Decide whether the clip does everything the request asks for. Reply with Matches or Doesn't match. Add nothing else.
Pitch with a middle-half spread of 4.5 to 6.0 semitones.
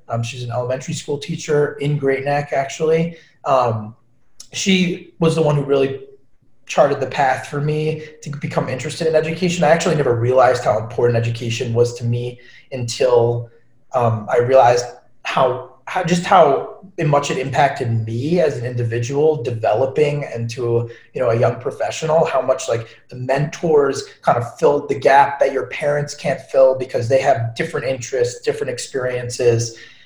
Matches